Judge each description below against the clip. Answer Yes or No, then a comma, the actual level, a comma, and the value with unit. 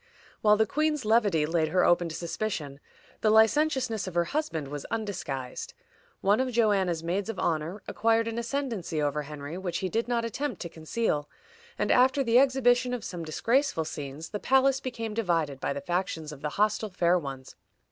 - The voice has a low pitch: No, high, 200 Hz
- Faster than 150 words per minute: Yes, average, 180 wpm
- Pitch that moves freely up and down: Yes, wide, 6.5 semitones